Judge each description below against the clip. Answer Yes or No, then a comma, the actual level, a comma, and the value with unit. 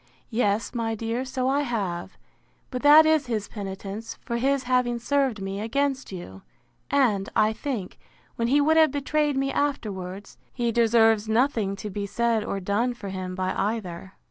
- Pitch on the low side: No, high, 230 Hz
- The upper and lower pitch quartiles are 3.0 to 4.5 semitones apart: No, average, 4.9 semitones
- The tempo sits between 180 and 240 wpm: No, average, 170 wpm